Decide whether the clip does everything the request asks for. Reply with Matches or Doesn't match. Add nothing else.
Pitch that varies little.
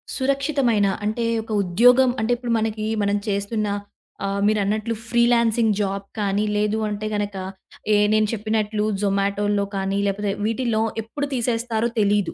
Matches